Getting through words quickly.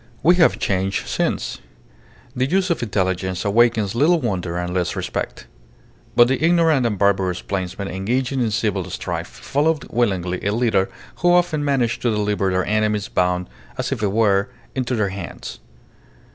No: average, 155 wpm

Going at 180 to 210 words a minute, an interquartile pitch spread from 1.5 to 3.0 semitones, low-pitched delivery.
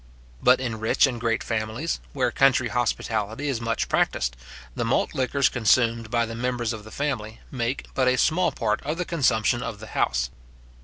Yes: average, 185 wpm; average, 2.7 semitones; low, 120 Hz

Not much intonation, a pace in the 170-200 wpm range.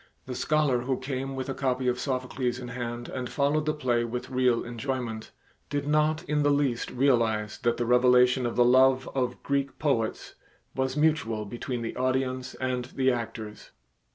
Yes: narrow, 2.0 semitones; average, 175 wpm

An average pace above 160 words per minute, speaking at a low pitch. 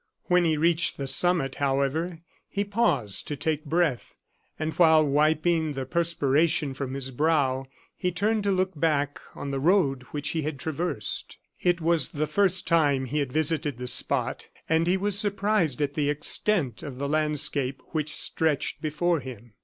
No: average, 170 wpm; medium, 155 Hz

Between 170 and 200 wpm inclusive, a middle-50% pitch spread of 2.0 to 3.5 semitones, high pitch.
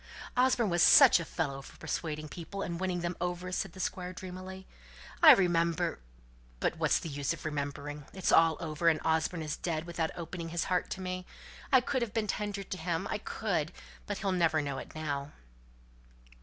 No: average, 185 wpm; average, 2.8 semitones; medium, 170 Hz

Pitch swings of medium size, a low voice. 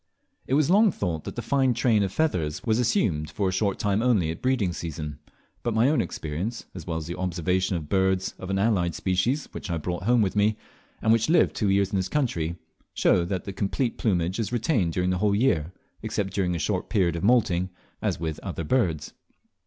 Yes: average, 4.8 semitones; very low, 95 Hz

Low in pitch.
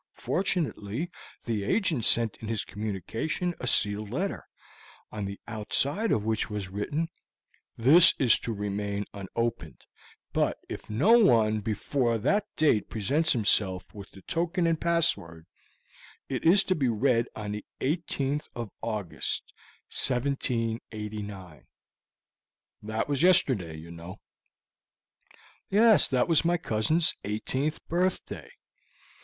Yes: low, 115 Hz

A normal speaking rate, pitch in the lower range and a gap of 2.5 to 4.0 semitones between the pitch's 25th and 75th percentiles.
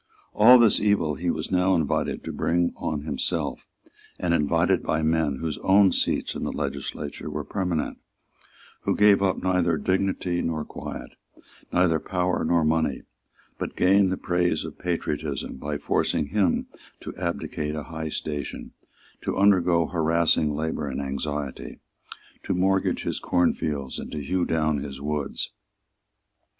Yes: average, 145 wpm; very low, 80 Hz; average, 3.3 semitones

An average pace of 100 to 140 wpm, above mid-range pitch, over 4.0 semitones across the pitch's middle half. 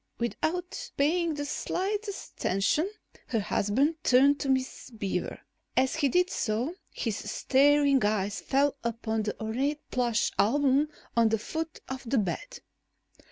Yes: slow, 135 wpm; very high, 265 Hz; average, 5.3 semitones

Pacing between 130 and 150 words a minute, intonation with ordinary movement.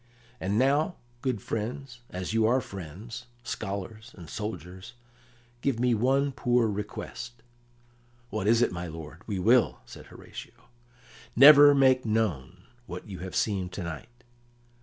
Yes: average, 140 wpm; average, 5.0 semitones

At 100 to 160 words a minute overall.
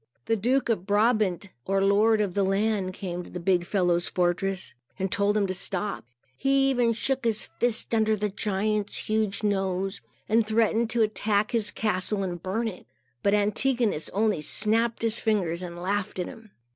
No: average, 175 wpm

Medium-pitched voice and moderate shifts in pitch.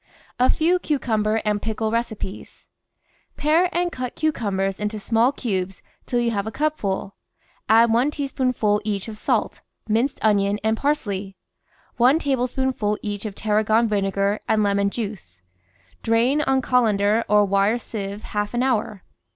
No: high, 220 Hz; average, 3.6 semitones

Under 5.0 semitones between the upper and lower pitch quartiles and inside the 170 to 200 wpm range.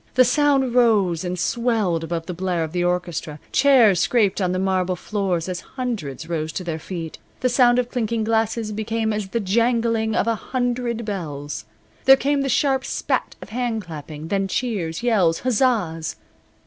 No: wide, 5.6 semitones; average, 175 wpm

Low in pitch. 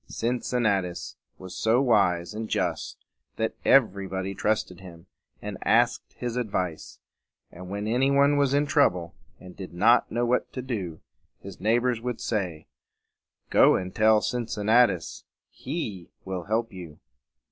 Yes: low, 110 Hz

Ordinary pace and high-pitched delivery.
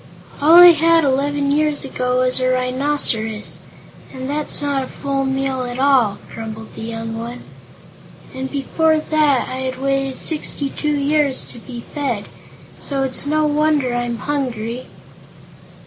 Yes: average, 145 wpm; very high, 270 Hz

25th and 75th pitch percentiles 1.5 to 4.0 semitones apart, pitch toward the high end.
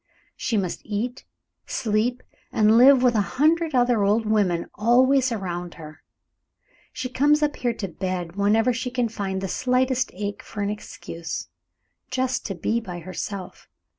No: average, 4.5 semitones; high, 225 Hz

